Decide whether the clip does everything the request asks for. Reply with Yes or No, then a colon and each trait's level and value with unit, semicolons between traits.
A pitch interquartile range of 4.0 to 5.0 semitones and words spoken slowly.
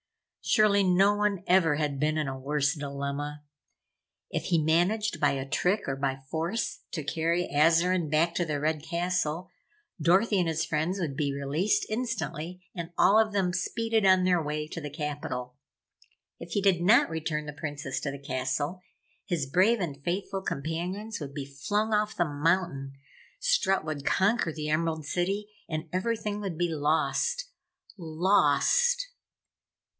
No: average, 4.6 semitones; average, 160 wpm